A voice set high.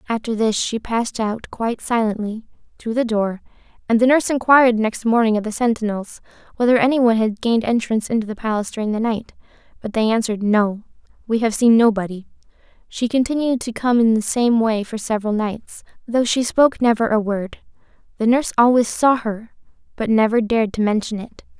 Yes: high, 225 Hz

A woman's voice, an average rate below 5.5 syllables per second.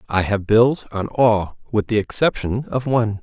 No: male; 4.6 syllables/s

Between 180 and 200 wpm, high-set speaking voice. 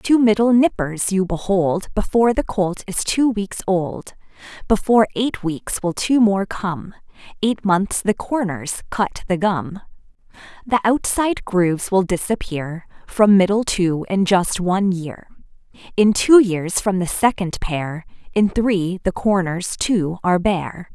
No: average, 150 wpm; high, 195 Hz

